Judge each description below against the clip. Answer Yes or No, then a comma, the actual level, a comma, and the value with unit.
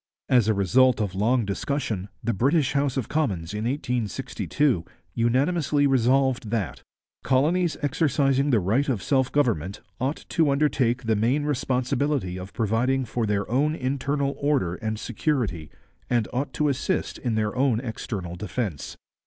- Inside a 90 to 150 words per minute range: Yes, average, 145 wpm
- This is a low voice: Yes, low, 125 Hz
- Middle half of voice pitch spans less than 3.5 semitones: No, average, 4.7 semitones